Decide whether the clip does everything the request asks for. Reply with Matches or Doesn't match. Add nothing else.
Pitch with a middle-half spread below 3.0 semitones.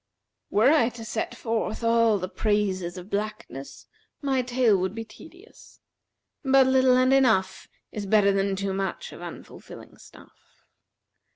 Doesn't match